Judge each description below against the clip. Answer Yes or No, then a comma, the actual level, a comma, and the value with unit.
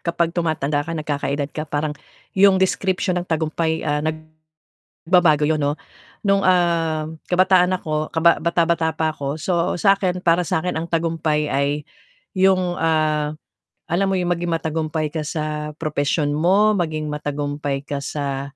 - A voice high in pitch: No, medium, 160 Hz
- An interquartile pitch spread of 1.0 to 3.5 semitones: Yes, average, 2.7 semitones